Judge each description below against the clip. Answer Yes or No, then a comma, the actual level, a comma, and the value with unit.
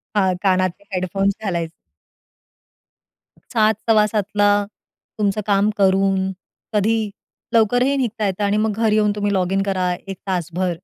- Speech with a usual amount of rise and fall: No, narrow, 2.1 semitones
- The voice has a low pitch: No, high, 200 Hz